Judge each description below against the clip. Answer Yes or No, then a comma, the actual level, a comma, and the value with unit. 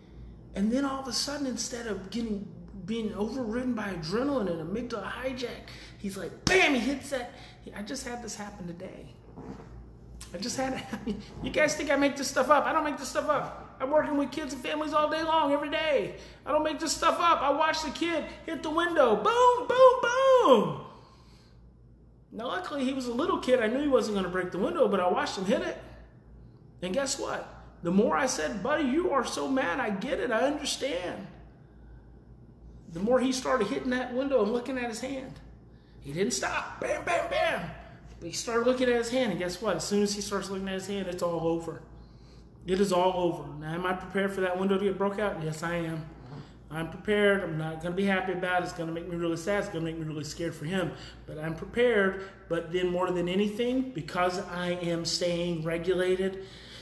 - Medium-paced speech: No, fast, 220 wpm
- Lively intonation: Yes, wide, 6.9 semitones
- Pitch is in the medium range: No, high, 210 Hz